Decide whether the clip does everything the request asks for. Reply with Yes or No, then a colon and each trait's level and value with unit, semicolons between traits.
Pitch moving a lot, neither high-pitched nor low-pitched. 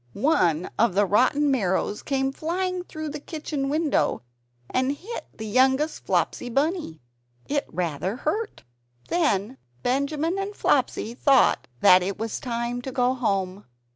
No: wide, 6.5 semitones; very high, 265 Hz